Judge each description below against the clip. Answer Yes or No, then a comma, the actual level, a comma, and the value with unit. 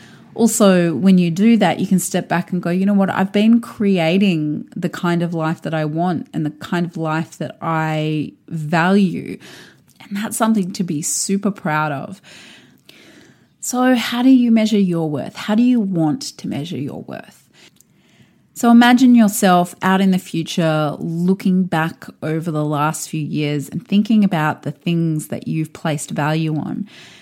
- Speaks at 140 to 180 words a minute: Yes, average, 175 wpm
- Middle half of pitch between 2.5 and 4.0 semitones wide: No, average, 4.4 semitones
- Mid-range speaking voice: Yes, medium, 180 Hz